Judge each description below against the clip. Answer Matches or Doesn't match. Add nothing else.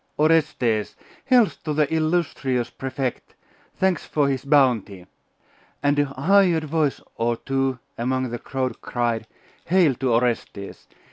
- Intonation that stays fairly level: Doesn't match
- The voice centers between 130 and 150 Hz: Matches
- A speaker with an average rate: Doesn't match